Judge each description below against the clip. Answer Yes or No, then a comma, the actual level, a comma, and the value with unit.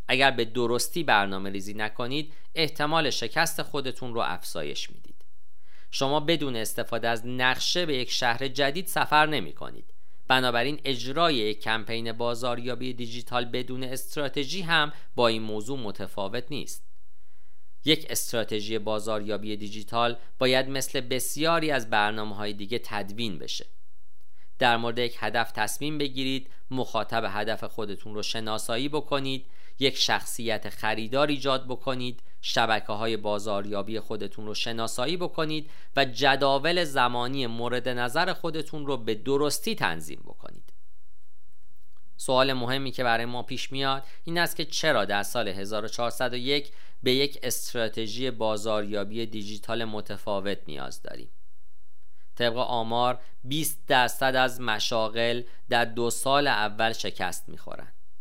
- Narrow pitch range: No, average, 4.1 semitones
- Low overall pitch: Yes, low, 120 Hz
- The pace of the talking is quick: No, average, 125 wpm